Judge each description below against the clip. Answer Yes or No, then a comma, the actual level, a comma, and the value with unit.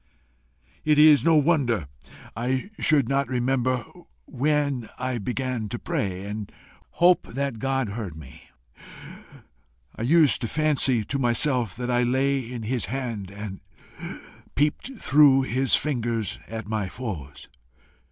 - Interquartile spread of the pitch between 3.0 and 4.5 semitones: Yes, average, 3.8 semitones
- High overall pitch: No, low, 125 Hz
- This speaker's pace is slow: Yes, slow, 130 wpm